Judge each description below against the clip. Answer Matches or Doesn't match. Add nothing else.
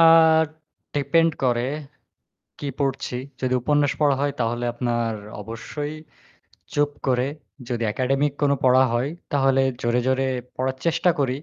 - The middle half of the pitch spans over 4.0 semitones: Doesn't match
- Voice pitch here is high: Doesn't match